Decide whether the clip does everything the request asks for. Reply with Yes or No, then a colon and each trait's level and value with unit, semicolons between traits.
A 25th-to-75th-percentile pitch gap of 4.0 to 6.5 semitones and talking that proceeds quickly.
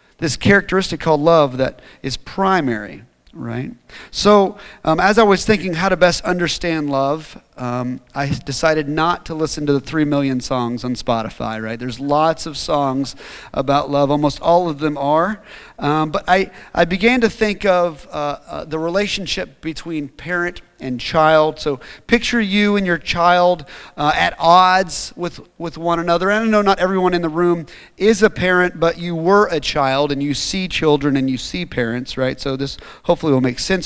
No: average, 4.5 semitones; average, 185 wpm